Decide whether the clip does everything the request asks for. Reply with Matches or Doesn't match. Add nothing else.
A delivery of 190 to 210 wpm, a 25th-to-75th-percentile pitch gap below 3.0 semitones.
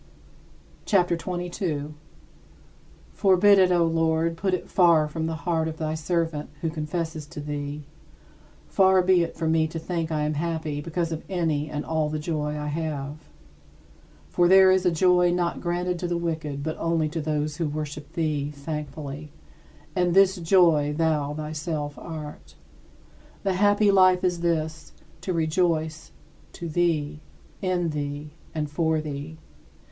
Doesn't match